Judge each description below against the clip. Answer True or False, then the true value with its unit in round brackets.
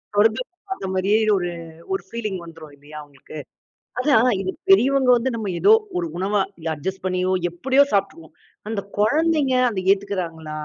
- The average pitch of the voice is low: False (200 Hz)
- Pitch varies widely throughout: True (6.5 semitones)